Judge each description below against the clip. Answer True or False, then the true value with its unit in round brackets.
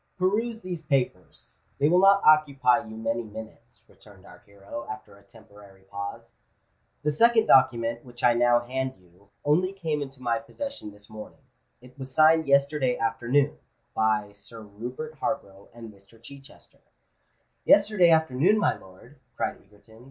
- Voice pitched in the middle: False (125 Hz)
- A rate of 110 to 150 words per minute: True (145 wpm)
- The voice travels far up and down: True (5.8 semitones)